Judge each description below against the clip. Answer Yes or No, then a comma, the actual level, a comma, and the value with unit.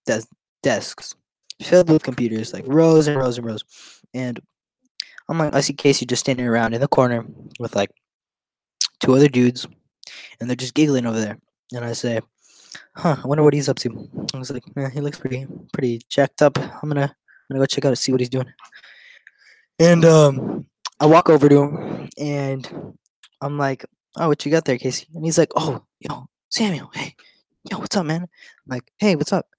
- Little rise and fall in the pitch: No, average, 3.8 semitones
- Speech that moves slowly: No, average, 200 wpm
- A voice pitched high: No, medium, 140 Hz